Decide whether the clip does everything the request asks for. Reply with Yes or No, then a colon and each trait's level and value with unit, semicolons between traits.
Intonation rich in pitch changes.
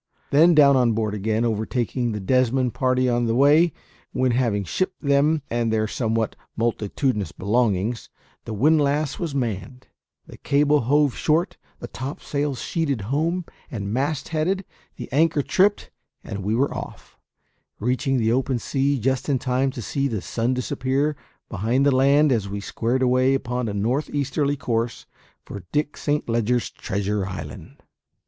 No: average, 4.0 semitones